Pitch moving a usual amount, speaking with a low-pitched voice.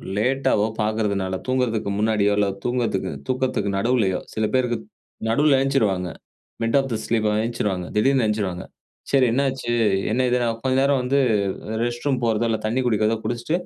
Yes: average, 3.5 semitones; low, 115 Hz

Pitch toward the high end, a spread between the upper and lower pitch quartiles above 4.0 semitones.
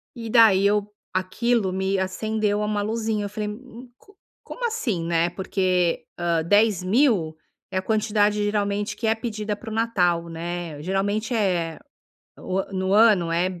No: high, 205 Hz; average, 3.1 semitones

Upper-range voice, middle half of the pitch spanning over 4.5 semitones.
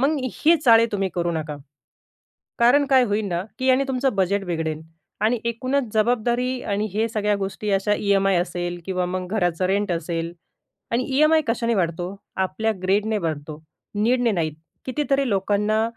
Yes: high, 210 Hz; average, 5.1 semitones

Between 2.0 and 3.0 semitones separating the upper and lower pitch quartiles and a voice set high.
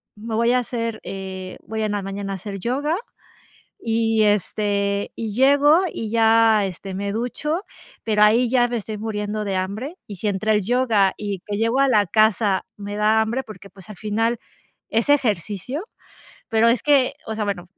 Yes: narrow, 2.5 semitones; high, 215 Hz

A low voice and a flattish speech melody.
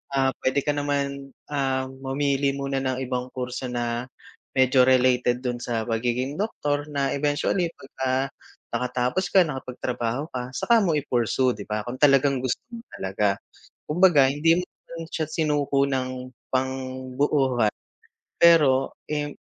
Yes: low, 130 Hz; narrow, 2.3 semitones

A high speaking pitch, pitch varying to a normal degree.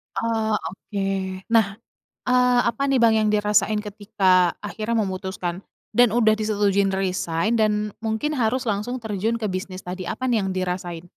Yes: high, 210 Hz; average, 3.1 semitones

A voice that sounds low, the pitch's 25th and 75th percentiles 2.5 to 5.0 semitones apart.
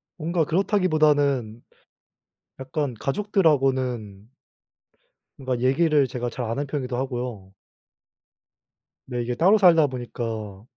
Yes: low, 130 Hz; average, 4.4 semitones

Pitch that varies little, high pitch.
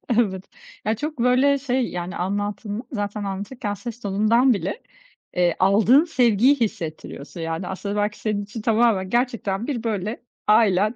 No: average, 3.6 semitones; high, 210 Hz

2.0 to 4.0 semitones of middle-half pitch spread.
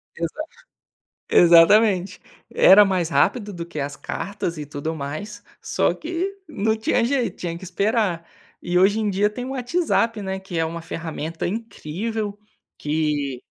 No: average, 4.9 semitones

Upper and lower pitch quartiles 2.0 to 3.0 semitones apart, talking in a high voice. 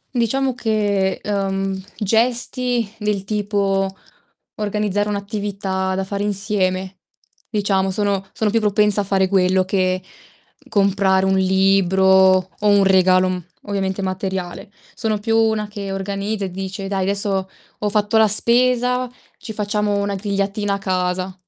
No: narrow, 1.6 semitones; high, 200 Hz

